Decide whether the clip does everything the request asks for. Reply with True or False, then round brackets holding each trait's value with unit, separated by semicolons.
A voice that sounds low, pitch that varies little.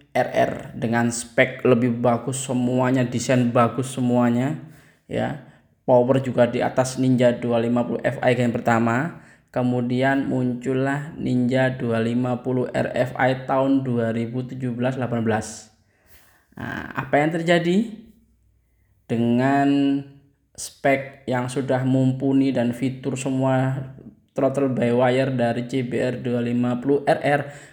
True (125 Hz; 2.0 semitones)